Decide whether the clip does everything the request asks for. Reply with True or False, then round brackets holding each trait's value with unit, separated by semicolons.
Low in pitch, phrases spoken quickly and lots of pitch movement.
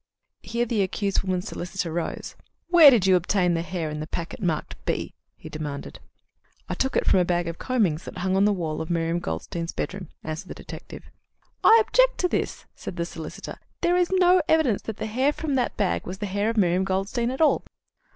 False (190 Hz; 210 wpm; 6.0 semitones)